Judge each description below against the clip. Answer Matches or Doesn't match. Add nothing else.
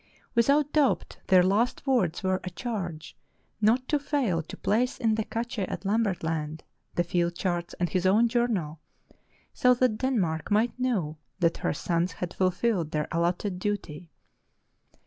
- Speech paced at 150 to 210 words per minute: Matches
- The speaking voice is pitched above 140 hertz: Matches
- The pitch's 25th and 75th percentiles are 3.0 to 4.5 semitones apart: Doesn't match